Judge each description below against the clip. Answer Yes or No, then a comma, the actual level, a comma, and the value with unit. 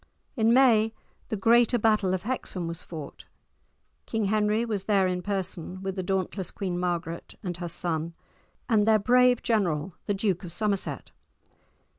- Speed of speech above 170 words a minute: No, average, 155 wpm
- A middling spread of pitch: Yes, average, 3.7 semitones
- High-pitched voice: Yes, high, 195 Hz